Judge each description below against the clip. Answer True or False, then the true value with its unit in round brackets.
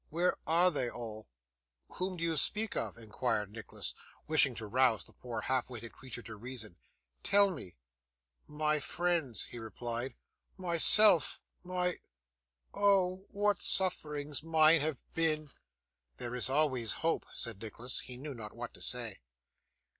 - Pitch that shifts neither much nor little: False (6.2 semitones)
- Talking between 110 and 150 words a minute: True (140 wpm)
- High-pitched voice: False (140 Hz)